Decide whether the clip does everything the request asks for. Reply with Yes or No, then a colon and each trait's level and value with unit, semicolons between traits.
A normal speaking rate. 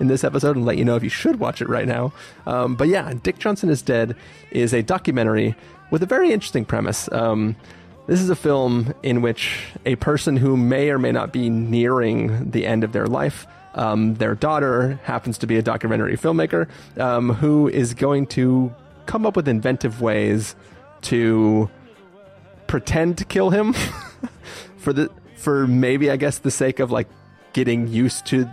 Yes: average, 185 wpm